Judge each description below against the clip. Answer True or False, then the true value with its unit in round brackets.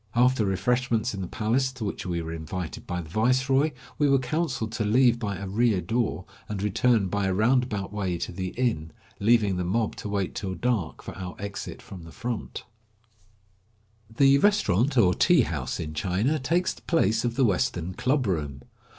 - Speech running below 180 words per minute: False (200 wpm)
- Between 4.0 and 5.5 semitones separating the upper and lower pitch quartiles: True (5.2 semitones)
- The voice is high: False (110 Hz)